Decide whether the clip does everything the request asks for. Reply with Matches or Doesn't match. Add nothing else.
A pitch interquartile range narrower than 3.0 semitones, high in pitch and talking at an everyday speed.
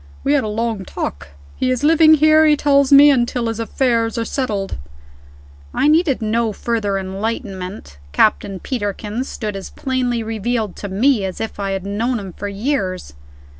Doesn't match